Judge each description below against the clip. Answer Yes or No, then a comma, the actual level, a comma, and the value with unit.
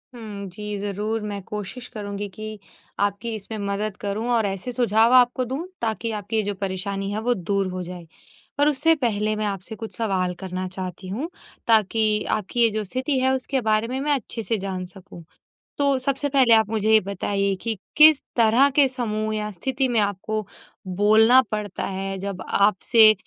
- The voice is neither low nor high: No, high, 215 Hz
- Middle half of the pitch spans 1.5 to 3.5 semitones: Yes, average, 3.0 semitones